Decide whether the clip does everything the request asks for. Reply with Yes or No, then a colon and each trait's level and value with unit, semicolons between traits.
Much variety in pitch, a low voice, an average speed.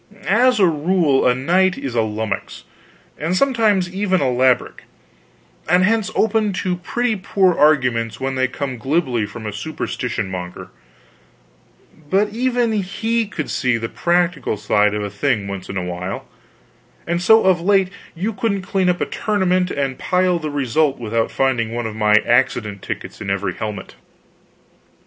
No: wide, 8.8 semitones; medium, 155 Hz; average, 165 wpm